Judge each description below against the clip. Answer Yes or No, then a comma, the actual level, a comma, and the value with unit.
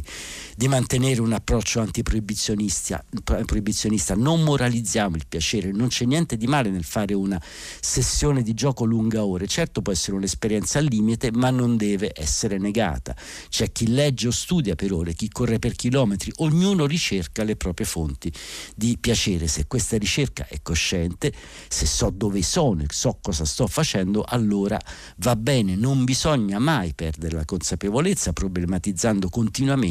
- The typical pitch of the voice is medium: No, low, 105 Hz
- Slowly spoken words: No, average, 155 wpm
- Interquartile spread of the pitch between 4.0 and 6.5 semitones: Yes, average, 4.7 semitones